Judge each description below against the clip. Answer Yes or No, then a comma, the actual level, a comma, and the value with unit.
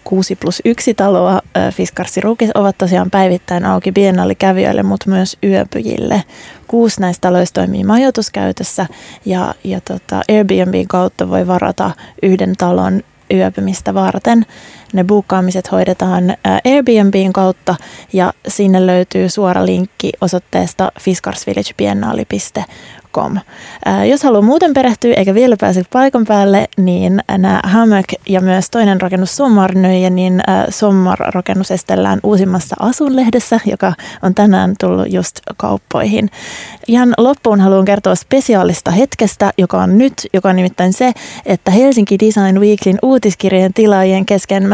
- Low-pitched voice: No, high, 195 Hz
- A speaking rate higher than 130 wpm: No, average, 125 wpm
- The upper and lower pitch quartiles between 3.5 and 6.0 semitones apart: No, average, 2.8 semitones